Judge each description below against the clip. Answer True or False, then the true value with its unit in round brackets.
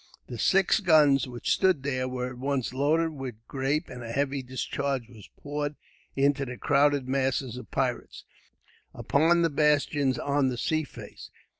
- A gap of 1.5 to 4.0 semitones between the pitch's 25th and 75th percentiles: True (2.4 semitones)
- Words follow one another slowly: False (160 wpm)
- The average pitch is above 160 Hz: False (140 Hz)